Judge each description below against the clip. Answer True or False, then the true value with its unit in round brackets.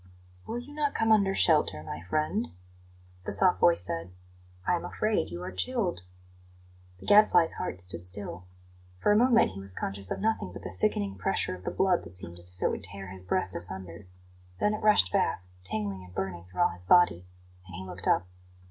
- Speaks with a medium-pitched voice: False (95 Hz)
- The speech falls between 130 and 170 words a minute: False (200 wpm)